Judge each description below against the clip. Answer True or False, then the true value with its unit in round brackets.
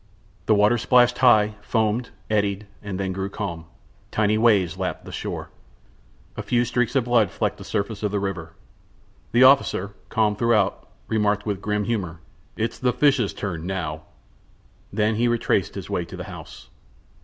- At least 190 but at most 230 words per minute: False (160 wpm)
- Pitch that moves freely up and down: False (3.0 semitones)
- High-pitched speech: False (105 Hz)